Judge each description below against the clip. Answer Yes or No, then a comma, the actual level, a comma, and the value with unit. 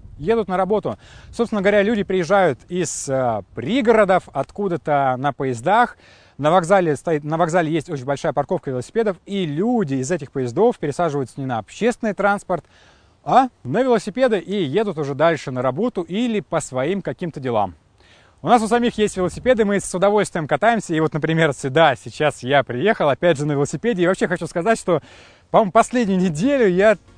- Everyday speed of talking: No, fast, 170 wpm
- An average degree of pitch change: No, wide, 6.4 semitones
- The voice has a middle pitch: Yes, medium, 180 Hz